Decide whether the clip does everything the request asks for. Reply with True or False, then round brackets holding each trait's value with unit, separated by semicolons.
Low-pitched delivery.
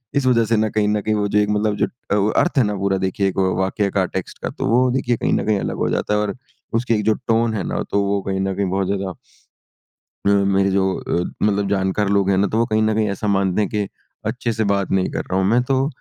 True (100 Hz)